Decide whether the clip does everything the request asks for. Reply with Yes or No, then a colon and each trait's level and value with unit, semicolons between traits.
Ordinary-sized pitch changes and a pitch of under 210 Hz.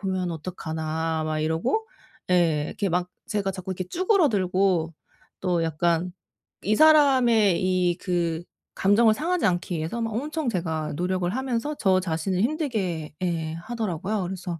Yes: average, 4.9 semitones; medium, 185 Hz